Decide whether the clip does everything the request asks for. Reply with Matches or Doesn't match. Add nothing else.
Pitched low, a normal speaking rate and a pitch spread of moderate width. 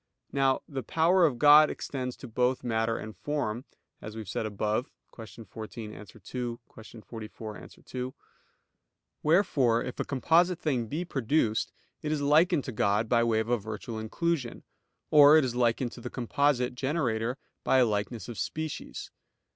Matches